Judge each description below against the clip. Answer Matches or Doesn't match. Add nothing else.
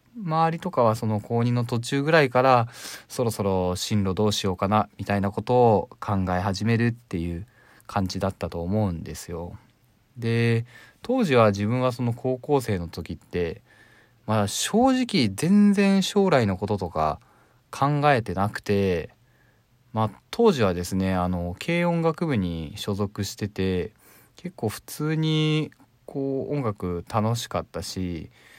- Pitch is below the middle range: Matches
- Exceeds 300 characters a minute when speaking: Doesn't match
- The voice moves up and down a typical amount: Doesn't match